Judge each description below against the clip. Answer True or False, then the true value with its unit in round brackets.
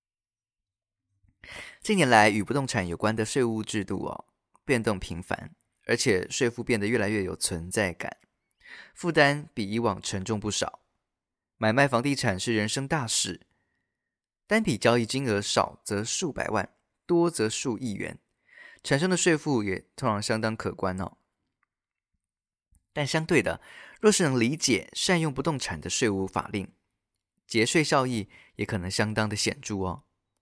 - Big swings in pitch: False (5.0 semitones)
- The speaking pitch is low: True (110 Hz)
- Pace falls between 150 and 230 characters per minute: True (220 characters per minute)